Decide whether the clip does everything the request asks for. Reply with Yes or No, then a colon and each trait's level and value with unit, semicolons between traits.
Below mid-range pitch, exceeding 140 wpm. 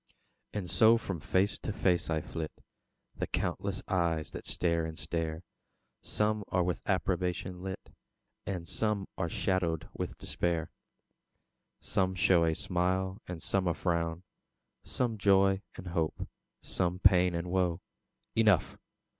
No: very low, 90 Hz; slow, 135 wpm